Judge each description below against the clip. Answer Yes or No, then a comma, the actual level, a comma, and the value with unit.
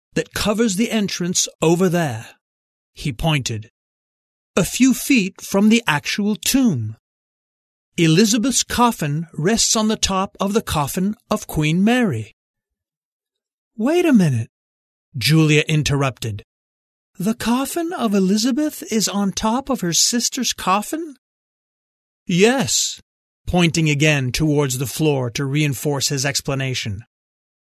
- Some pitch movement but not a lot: No, wide, 8.3 semitones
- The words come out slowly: Yes, slow, 115 wpm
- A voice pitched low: No, medium, 175 Hz